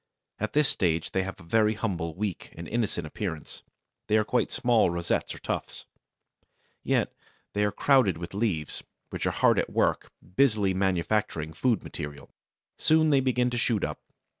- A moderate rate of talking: Yes, average, 165 wpm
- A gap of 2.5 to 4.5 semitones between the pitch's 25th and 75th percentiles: No, average, 5.3 semitones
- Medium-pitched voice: No, low, 105 Hz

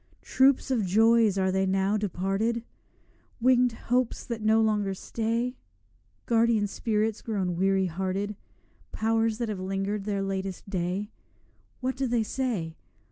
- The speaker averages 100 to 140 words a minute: Yes, slow, 135 wpm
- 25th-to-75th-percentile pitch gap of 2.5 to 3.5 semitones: Yes, average, 3.1 semitones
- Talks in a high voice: Yes, high, 210 Hz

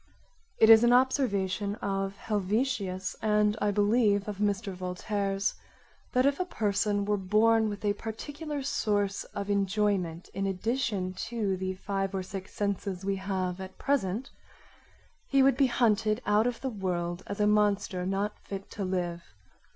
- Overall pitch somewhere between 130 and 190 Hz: No, high, 205 Hz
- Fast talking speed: No, average, 155 wpm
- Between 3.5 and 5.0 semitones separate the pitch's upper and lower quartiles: No, narrow, 2.5 semitones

